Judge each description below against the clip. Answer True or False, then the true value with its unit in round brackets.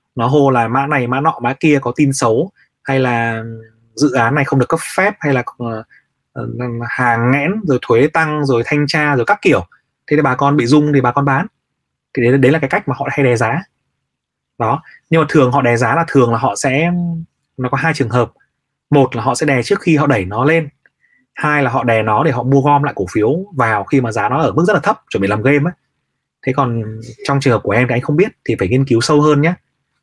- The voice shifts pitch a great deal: False (3.7 semitones)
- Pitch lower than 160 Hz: True (135 Hz)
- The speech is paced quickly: True (255 wpm)